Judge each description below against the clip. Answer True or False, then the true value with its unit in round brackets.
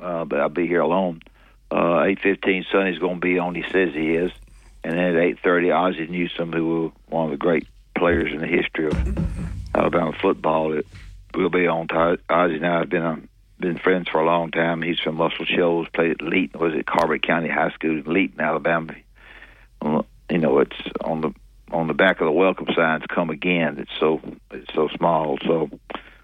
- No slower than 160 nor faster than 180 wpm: False (205 wpm)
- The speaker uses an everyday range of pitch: False (1.6 semitones)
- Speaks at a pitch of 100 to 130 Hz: False (85 Hz)